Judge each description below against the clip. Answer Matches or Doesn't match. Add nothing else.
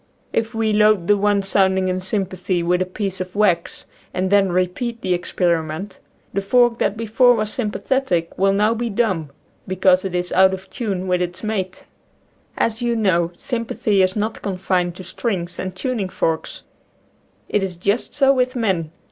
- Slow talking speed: Doesn't match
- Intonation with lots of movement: Doesn't match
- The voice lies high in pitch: Matches